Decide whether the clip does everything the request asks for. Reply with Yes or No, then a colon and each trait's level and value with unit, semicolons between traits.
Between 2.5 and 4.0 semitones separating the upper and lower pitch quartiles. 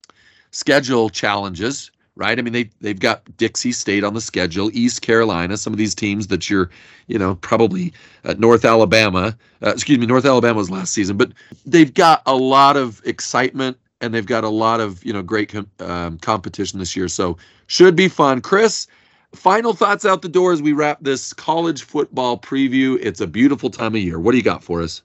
No: average, 4.6 semitones